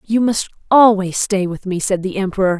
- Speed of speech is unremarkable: No, fast, 210 wpm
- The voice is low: No, high, 195 Hz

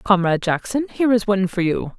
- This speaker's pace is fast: Yes, fast, 210 wpm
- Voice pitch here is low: No, high, 205 Hz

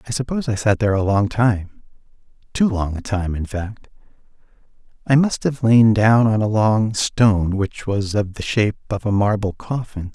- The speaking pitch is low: Yes, low, 105 Hz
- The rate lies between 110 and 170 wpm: No, average, 185 wpm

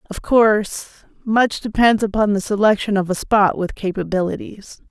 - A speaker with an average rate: Yes, average, 145 wpm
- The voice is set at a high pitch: Yes, high, 205 Hz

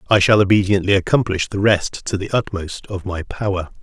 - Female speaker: No, male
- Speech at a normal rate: Yes, average, 190 wpm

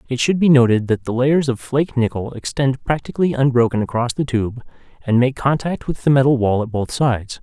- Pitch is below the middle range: Yes, low, 130 Hz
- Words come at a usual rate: No, fast, 210 wpm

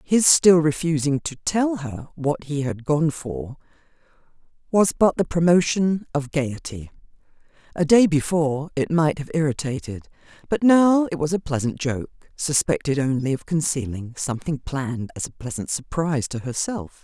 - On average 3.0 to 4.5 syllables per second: No, 4.8 syllables/s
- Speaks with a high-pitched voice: No, medium, 150 Hz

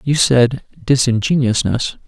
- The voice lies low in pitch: Yes, low, 125 Hz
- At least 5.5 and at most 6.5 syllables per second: No, 3.9 syllables/s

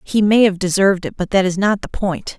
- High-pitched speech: Yes, high, 195 Hz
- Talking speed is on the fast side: Yes, fast, 275 wpm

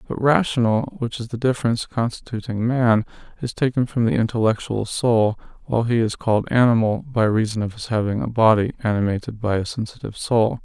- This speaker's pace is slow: No, average, 175 wpm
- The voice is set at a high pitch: No, low, 115 Hz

